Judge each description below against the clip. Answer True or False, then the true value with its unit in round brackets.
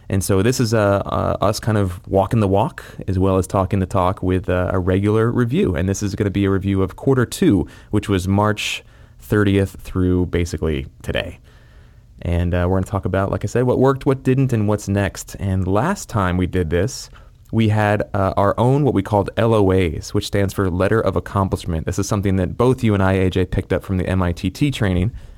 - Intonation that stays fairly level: True (2.3 semitones)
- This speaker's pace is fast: True (220 wpm)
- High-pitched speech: False (100 Hz)